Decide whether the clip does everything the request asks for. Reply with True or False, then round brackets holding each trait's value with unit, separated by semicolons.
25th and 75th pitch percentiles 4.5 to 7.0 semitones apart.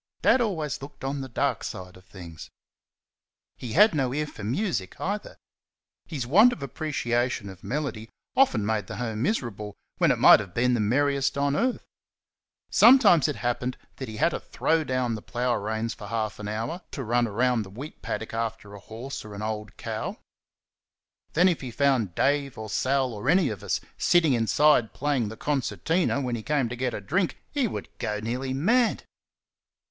True (5.2 semitones)